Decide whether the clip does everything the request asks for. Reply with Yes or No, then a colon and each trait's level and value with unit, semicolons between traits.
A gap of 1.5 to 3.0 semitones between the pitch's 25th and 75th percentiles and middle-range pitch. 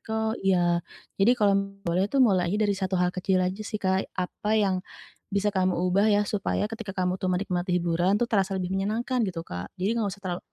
No: narrow, 2.4 semitones; high, 195 Hz